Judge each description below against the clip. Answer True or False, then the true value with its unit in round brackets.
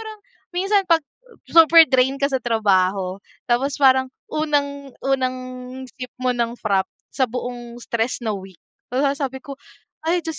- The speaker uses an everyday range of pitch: True (3.3 semitones)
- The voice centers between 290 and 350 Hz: False (260 Hz)